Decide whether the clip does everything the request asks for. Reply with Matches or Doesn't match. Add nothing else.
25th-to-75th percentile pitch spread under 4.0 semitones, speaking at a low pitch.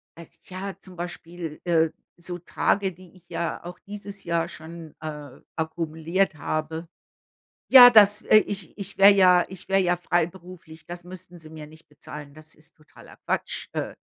Doesn't match